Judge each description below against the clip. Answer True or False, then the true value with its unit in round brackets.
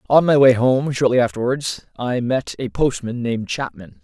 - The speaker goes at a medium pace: True (180 wpm)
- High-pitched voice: False (120 Hz)